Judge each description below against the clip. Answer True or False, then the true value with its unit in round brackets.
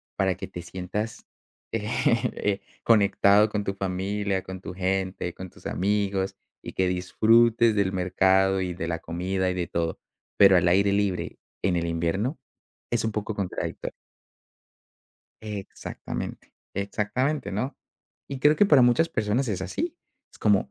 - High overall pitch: False (100 Hz)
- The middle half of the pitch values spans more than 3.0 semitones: False (2.7 semitones)